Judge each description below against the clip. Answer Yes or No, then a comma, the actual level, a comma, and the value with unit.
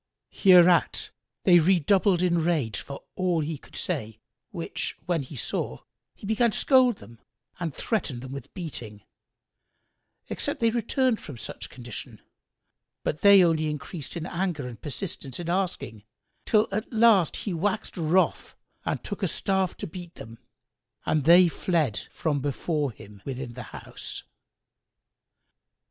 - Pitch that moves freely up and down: Yes, wide, 5.9 semitones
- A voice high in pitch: No, medium, 165 Hz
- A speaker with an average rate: Yes, average, 145 wpm